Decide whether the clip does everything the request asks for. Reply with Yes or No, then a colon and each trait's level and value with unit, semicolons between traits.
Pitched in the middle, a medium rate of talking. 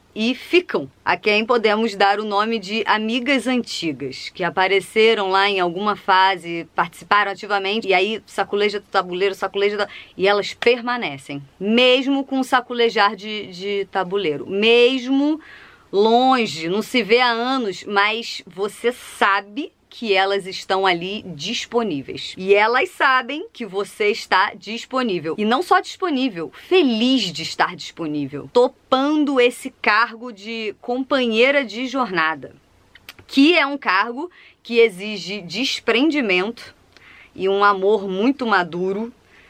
No: high, 215 Hz; average, 130 wpm